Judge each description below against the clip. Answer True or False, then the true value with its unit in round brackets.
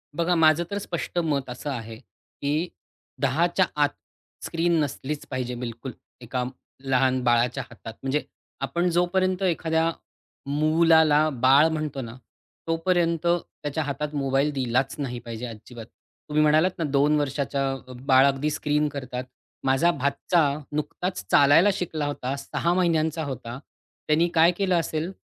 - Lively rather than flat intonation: False (3.8 semitones)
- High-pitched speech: False (145 Hz)